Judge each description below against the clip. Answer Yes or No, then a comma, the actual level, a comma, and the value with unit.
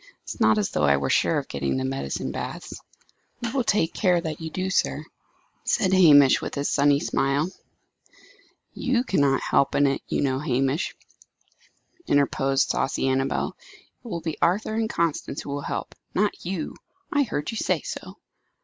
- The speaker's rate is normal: Yes, average, 180 wpm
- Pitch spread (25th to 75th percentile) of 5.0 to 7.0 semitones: Yes, wide, 5.6 semitones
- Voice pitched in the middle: Yes, medium, 145 Hz